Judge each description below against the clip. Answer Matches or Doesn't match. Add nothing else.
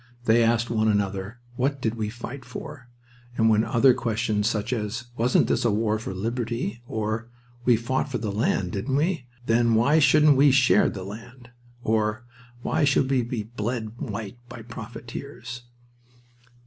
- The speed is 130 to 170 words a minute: Matches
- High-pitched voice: Doesn't match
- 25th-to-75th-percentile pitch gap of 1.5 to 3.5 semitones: Matches